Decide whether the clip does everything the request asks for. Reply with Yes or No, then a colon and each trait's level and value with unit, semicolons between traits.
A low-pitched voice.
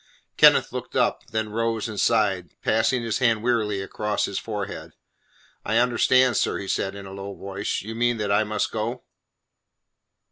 Yes: low, 110 Hz